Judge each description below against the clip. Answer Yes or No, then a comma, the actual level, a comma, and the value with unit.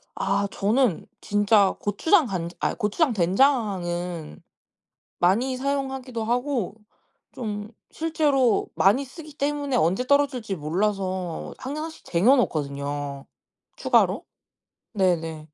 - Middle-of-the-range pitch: No, high, 210 Hz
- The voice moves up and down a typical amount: No, wide, 6.9 semitones